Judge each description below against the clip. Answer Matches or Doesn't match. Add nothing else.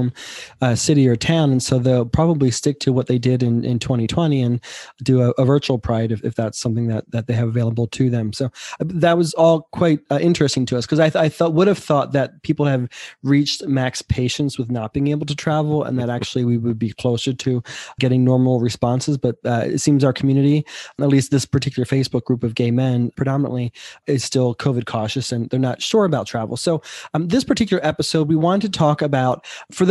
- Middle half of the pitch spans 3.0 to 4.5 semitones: Matches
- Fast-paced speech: Matches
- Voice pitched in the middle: Doesn't match